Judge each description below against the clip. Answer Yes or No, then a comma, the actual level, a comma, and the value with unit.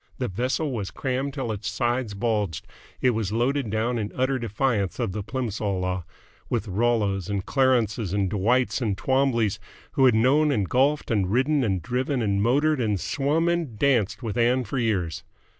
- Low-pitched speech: Yes, low, 115 Hz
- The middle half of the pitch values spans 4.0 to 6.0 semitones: Yes, average, 4.3 semitones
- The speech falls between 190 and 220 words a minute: No, average, 175 wpm